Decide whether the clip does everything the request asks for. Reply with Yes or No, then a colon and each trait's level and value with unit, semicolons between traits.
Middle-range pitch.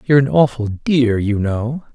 No: low, 125 Hz